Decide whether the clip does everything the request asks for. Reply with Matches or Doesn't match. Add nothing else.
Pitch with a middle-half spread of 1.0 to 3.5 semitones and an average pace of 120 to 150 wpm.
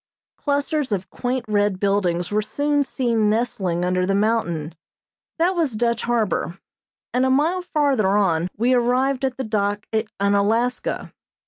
Doesn't match